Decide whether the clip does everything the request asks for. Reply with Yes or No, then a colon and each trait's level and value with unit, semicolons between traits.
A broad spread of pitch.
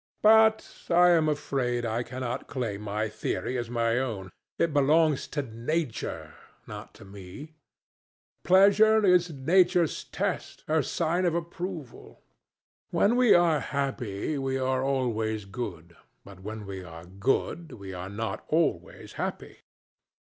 Yes: wide, 7.5 semitones